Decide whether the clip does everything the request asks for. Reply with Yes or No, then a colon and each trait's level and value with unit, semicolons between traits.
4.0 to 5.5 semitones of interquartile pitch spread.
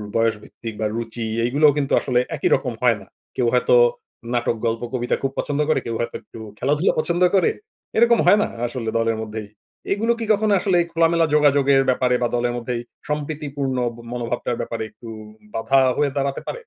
Yes: average, 4.3 semitones